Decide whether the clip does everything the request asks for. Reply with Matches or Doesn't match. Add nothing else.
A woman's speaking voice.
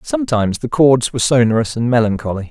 Doesn't match